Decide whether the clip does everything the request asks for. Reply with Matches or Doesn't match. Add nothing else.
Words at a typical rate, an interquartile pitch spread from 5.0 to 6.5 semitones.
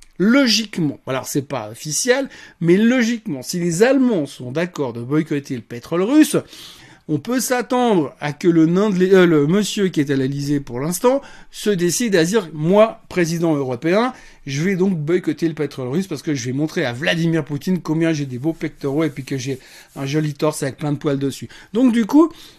Matches